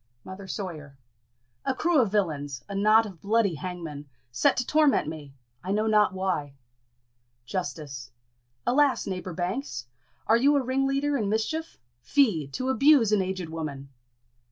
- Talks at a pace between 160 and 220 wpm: No, average, 145 wpm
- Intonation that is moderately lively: No, wide, 8.1 semitones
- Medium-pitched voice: No, high, 195 Hz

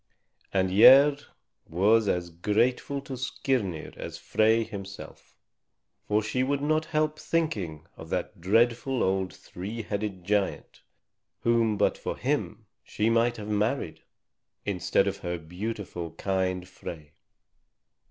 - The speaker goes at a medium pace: No, slow, 125 wpm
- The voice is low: Yes, low, 105 Hz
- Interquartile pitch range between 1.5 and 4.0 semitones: No, average, 4.5 semitones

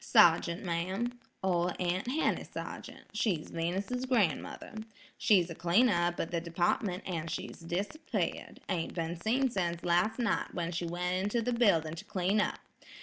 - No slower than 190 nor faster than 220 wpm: No, average, 155 wpm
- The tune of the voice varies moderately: Yes, average, 4.2 semitones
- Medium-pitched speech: Yes, medium, 180 Hz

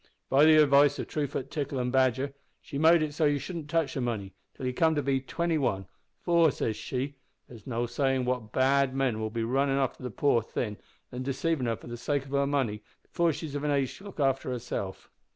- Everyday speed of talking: No, fast, 235 wpm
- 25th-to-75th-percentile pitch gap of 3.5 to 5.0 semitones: No, average, 2.8 semitones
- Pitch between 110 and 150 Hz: Yes, low, 135 Hz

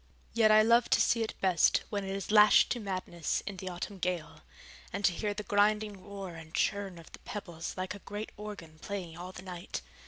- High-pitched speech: Yes, high, 195 Hz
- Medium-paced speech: No, fast, 215 wpm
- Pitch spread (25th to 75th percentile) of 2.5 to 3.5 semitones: Yes, average, 2.8 semitones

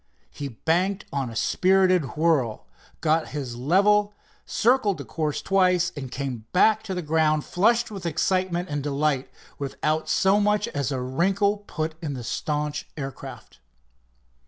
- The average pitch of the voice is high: No, medium, 160 Hz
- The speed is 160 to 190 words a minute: No, average, 145 wpm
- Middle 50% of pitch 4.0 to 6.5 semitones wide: Yes, average, 5.3 semitones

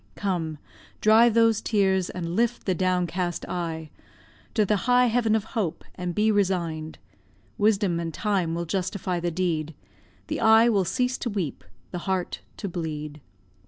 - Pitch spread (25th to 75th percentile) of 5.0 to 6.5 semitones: No, average, 4.1 semitones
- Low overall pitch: No, medium, 185 Hz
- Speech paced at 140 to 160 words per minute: Yes, average, 155 wpm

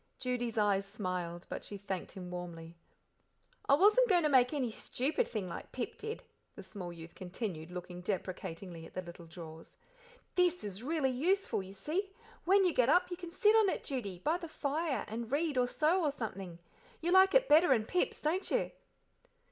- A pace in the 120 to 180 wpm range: No, average, 190 wpm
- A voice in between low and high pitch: No, high, 245 Hz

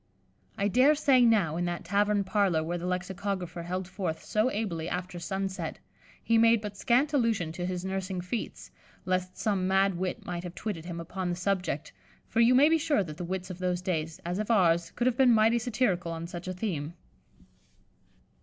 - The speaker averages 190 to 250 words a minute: Yes, average, 200 wpm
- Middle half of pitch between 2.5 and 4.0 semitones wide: Yes, average, 3.7 semitones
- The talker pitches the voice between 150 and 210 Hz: Yes, medium, 185 Hz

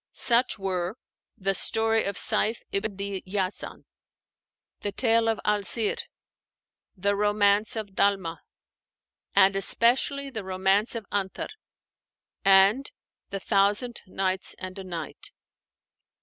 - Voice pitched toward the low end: No, high, 200 Hz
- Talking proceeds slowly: Yes, slow, 115 wpm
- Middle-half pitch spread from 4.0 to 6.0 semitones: No, narrow, 2.4 semitones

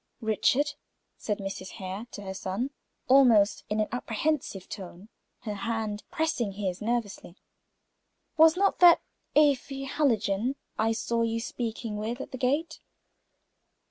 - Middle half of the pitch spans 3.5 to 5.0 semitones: Yes, average, 4.7 semitones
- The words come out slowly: Yes, slow, 130 wpm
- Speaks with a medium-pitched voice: No, high, 225 Hz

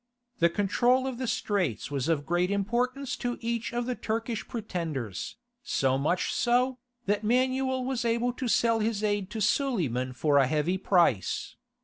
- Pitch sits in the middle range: No, high, 215 Hz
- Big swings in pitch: Yes, wide, 6.3 semitones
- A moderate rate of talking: Yes, average, 160 wpm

